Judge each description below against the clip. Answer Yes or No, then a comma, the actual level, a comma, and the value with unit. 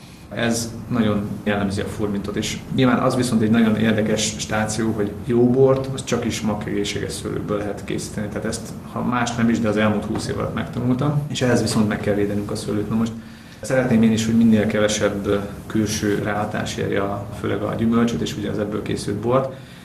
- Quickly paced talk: Yes, fast, 195 wpm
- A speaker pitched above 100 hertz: Yes, low, 110 Hz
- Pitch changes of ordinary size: No, narrow, 2.0 semitones